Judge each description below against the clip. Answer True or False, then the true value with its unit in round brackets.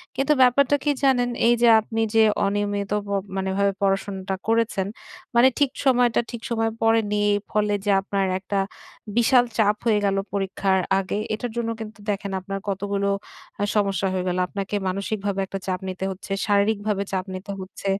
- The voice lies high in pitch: True (205 Hz)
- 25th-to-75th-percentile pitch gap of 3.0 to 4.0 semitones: False (2.5 semitones)